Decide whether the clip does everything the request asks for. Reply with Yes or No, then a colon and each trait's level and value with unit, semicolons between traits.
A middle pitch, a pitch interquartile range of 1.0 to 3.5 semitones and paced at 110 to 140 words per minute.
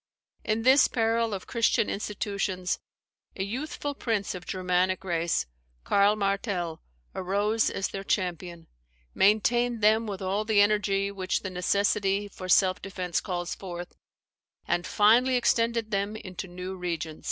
No: high, 195 Hz; average, 2.8 semitones; slow, 135 wpm